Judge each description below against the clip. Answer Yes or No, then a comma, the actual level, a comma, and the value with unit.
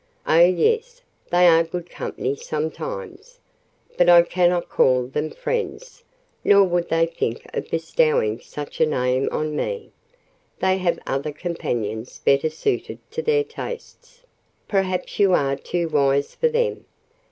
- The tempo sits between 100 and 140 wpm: Yes, slow, 135 wpm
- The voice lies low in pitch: No, medium, 175 Hz